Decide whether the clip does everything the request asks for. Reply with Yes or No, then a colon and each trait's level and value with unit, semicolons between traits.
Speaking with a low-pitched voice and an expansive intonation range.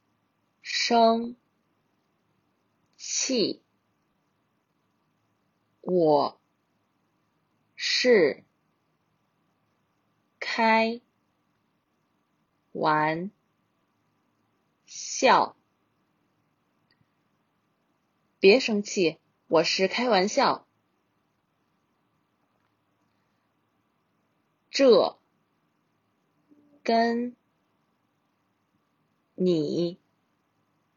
No: high, 225 Hz; wide, 6.8 semitones